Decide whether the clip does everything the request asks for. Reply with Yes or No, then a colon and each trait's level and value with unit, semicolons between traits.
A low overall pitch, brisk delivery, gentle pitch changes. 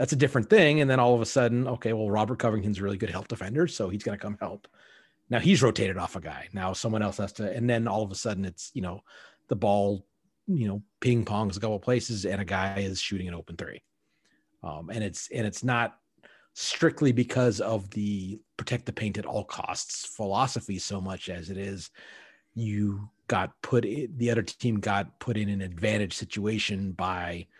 No: low, 105 Hz; fast, 215 wpm; average, 3.2 semitones